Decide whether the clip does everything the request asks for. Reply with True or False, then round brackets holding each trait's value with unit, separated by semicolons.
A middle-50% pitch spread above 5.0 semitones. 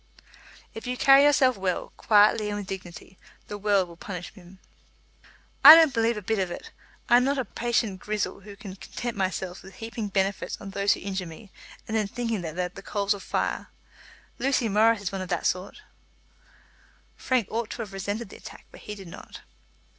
False (3.2 semitones)